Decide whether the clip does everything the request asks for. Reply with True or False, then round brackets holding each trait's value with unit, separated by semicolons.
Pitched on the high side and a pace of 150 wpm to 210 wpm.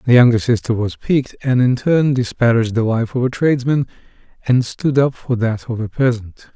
False (120 Hz; 200 wpm)